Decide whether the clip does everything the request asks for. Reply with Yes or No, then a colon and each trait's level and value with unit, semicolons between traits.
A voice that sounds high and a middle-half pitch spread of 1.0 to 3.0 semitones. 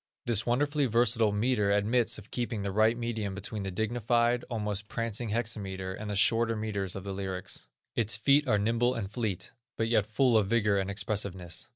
No: low, 110 Hz; average, 2.7 semitones